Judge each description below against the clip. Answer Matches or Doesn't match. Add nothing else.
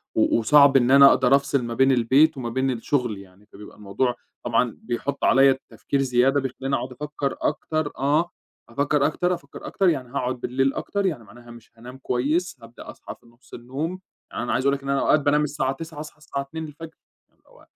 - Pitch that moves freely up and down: Doesn't match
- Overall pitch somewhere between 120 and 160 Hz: Matches